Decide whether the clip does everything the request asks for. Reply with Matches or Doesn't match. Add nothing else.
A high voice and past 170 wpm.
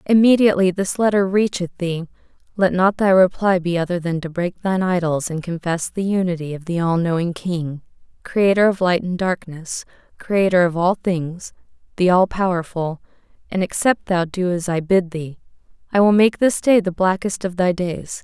Doesn't match